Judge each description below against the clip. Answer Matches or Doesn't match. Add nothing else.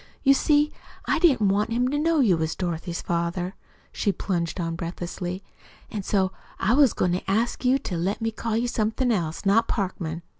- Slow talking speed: Doesn't match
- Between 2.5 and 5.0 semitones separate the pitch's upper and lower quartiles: Doesn't match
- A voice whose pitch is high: Matches